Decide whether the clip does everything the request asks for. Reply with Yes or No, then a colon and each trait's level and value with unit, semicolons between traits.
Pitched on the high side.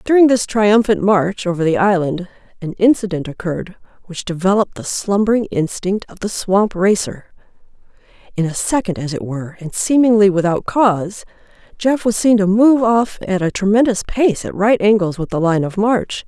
Yes: high, 200 Hz